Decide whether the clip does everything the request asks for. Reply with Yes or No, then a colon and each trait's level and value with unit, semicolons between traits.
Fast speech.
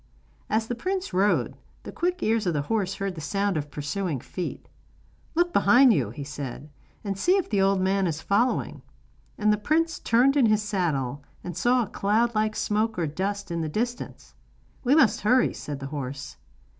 No: average, 190 wpm